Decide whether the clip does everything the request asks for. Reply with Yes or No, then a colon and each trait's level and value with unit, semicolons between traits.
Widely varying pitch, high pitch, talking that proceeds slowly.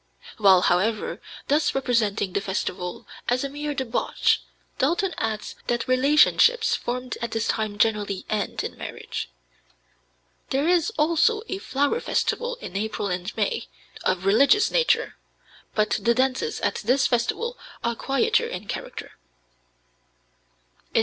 Yes: wide, 6.6 semitones; very high, 250 Hz; slow, 130 wpm